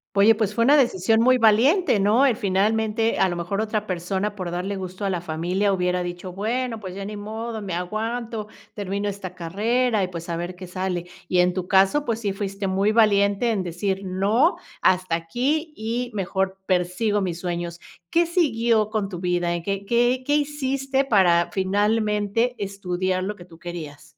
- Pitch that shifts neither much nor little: Yes, average, 3.7 semitones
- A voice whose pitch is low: No, high, 200 Hz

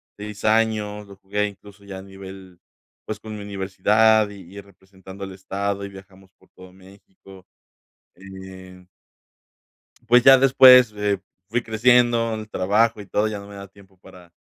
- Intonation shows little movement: Yes, narrow, 2.1 semitones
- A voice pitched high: No, low, 100 Hz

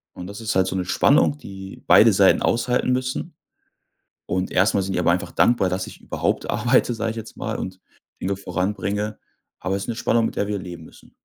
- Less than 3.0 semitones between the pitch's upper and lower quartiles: No, average, 3.5 semitones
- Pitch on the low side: Yes, low, 100 Hz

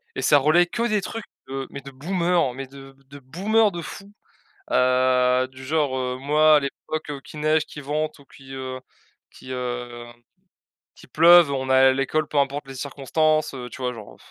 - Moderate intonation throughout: Yes, average, 3.1 semitones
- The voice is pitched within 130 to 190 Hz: Yes, medium, 140 Hz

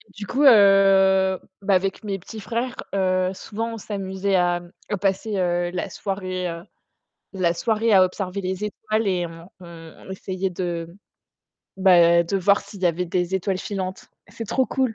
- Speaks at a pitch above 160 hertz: Yes, high, 190 Hz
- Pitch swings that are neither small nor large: No, narrow, 2.1 semitones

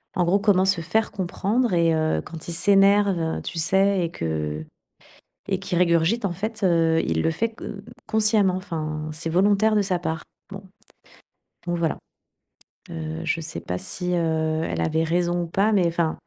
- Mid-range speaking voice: Yes, medium, 175 Hz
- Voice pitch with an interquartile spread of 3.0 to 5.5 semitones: Yes, average, 3.5 semitones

